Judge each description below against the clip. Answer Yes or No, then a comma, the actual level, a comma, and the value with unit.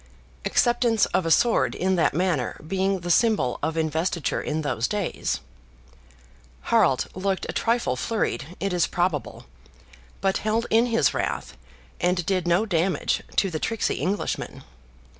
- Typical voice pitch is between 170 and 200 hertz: Yes, medium, 185 Hz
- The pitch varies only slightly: No, average, 4.3 semitones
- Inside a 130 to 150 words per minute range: Yes, average, 140 wpm